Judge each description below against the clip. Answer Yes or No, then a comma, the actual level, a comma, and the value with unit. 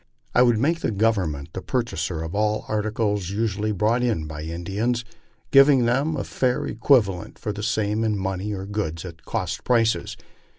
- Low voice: Yes, low, 105 Hz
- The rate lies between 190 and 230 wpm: No, average, 170 wpm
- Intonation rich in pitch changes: No, average, 4.0 semitones